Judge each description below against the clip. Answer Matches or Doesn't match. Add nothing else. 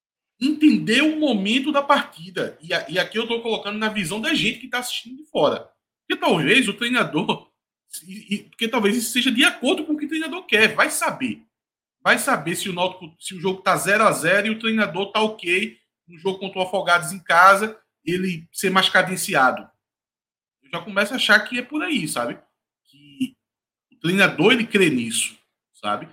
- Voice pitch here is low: Doesn't match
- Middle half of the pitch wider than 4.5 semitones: Matches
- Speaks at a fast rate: Matches